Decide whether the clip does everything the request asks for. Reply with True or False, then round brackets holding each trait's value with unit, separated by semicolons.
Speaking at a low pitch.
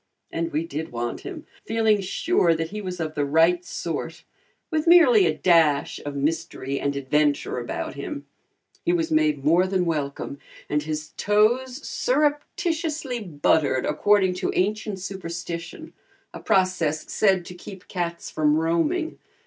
False (170 Hz)